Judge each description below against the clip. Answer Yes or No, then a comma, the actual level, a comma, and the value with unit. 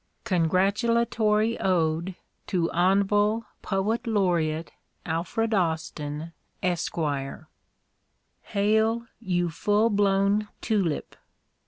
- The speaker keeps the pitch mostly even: No, average, 4.3 semitones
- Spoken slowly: Yes, slow, 70 wpm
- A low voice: No, high, 195 Hz